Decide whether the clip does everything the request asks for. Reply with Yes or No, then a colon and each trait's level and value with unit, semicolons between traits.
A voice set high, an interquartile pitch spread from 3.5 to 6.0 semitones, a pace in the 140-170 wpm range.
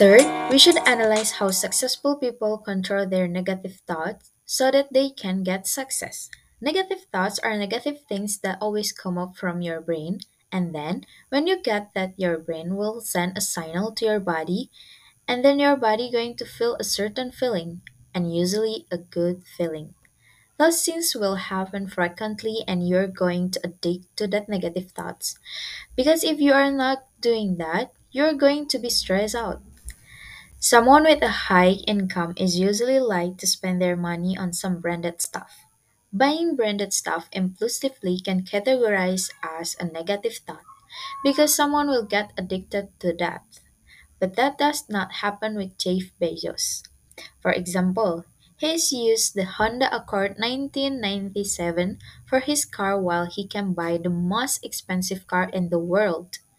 Yes: high, 200 Hz; average, 5.2 semitones; average, 160 wpm